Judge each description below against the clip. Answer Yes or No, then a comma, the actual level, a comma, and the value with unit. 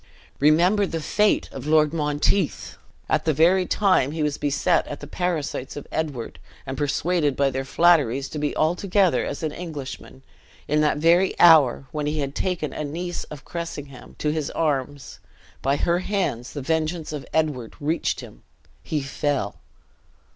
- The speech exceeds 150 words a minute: Yes, average, 160 wpm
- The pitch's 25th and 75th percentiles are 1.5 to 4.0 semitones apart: Yes, average, 3.1 semitones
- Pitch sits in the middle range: Yes, medium, 150 Hz